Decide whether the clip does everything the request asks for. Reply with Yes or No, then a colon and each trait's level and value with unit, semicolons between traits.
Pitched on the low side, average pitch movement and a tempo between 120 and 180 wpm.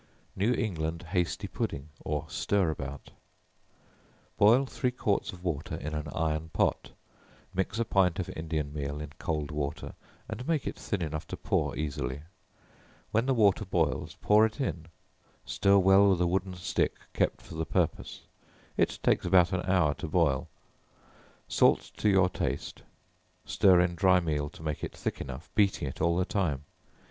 Yes: very low, 85 Hz; average, 4.2 semitones; average, 165 wpm